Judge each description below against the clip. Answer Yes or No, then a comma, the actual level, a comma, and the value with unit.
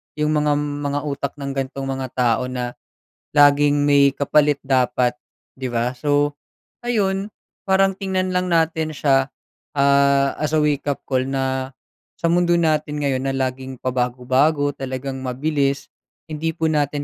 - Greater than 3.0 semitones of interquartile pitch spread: No, narrow, 2.5 semitones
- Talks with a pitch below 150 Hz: Yes, medium, 140 Hz